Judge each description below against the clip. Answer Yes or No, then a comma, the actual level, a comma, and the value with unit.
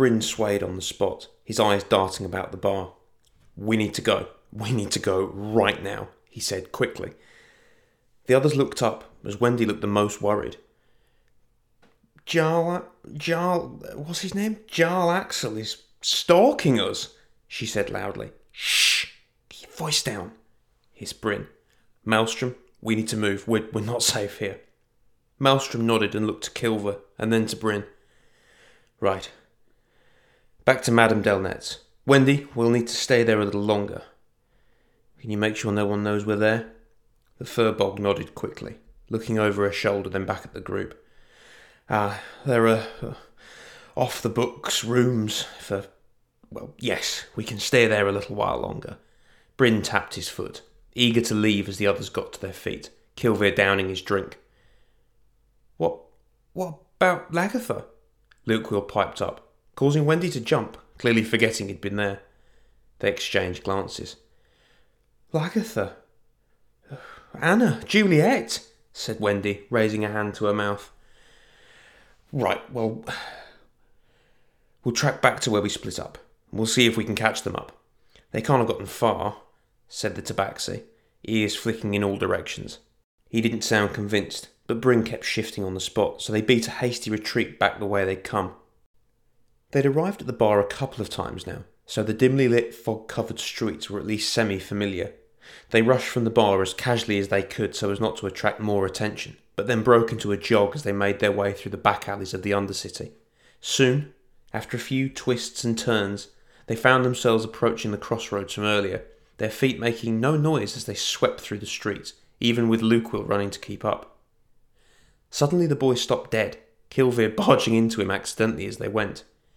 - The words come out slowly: No, average, 165 wpm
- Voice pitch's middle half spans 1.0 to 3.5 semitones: Yes, average, 3.2 semitones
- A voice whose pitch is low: Yes, low, 110 Hz